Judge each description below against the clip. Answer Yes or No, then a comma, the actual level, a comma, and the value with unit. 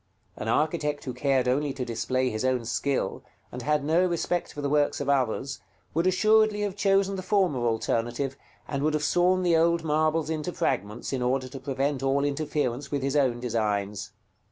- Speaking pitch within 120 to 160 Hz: Yes, medium, 140 Hz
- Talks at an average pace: Yes, average, 185 wpm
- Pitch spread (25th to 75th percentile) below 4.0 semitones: No, average, 4.3 semitones